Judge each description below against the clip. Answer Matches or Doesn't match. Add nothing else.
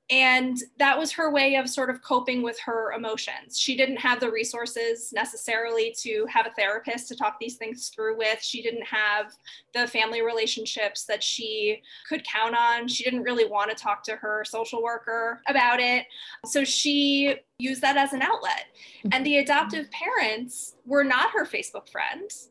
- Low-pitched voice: Doesn't match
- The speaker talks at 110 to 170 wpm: Doesn't match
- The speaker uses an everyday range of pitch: Matches